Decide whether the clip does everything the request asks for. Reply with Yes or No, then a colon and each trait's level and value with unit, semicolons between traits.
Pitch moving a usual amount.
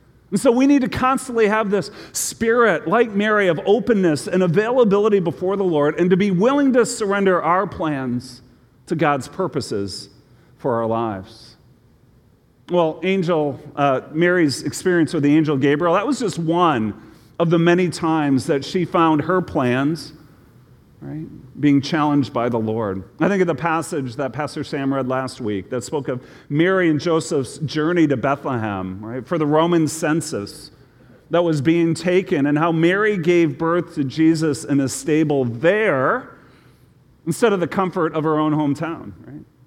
Yes: average, 4.8 semitones